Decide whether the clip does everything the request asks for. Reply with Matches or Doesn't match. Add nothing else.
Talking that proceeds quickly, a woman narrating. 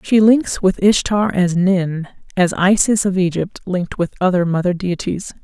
Doesn't match